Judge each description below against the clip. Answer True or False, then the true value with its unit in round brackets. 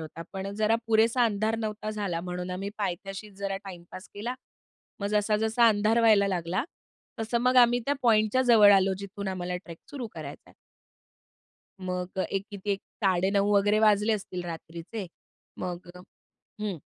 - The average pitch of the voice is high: True (200 Hz)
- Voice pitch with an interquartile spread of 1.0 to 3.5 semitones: True (2.8 semitones)